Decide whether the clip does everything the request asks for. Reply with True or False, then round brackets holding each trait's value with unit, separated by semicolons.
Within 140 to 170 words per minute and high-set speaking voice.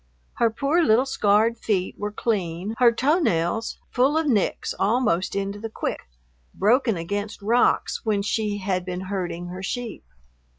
True (155 wpm; 210 Hz)